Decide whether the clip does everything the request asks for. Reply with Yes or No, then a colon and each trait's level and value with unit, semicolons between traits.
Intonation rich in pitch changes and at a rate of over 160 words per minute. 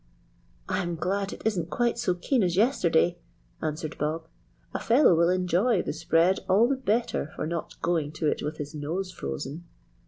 No: average, 3.8 semitones; average, 175 wpm